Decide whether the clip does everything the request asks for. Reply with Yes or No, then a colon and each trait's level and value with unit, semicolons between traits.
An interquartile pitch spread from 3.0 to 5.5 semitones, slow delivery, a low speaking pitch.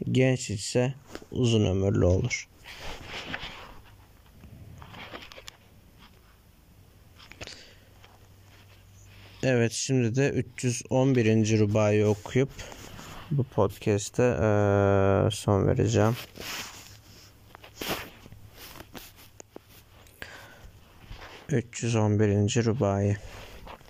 No: narrow, 2.6 semitones; slow, 45 wpm; low, 105 Hz